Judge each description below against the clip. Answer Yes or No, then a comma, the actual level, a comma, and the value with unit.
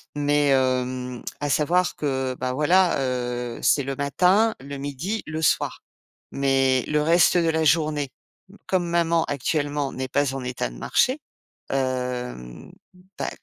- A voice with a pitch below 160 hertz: Yes, medium, 140 Hz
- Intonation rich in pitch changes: No, average, 3.8 semitones